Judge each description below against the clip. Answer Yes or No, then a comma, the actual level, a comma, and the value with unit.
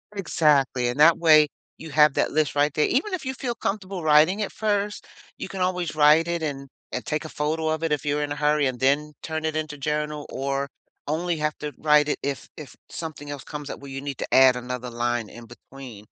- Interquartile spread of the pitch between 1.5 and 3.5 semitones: Yes, average, 2.7 semitones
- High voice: No, medium, 150 Hz